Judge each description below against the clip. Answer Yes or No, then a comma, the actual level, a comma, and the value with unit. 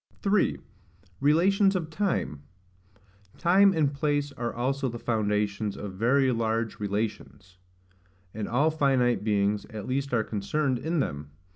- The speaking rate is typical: No, slow, 130 wpm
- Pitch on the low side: Yes, low, 125 Hz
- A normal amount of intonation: No, wide, 6.1 semitones